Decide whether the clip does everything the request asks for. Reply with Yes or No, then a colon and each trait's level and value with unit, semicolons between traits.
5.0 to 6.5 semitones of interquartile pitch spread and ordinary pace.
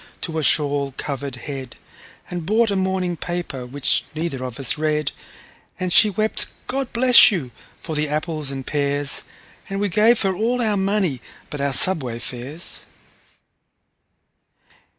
Yes: wide, 5.6 semitones; average, 150 wpm